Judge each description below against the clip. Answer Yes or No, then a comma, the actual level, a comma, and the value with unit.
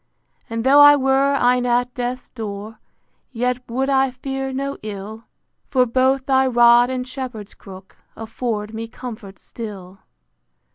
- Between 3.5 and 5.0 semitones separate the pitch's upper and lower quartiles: No, average, 3.0 semitones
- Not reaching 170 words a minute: Yes, average, 140 wpm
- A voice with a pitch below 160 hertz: No, high, 245 Hz